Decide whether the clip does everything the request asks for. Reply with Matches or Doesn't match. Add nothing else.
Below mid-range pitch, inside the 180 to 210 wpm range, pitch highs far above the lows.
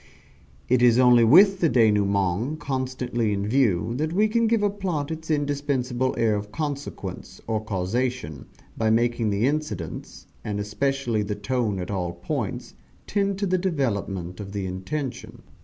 Doesn't match